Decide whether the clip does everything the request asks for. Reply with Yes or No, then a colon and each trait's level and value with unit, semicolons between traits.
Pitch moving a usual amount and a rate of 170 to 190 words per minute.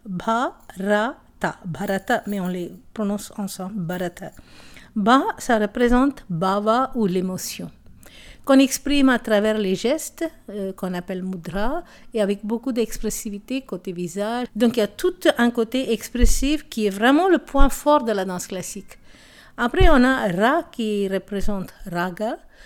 No: average, 5.0 semitones; slow, 145 wpm